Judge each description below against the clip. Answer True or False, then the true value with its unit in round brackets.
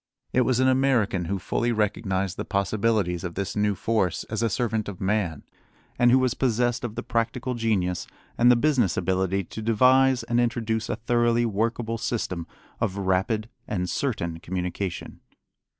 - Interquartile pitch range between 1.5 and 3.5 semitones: False (3.9 semitones)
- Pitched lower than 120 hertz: True (110 Hz)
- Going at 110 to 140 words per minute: False (165 wpm)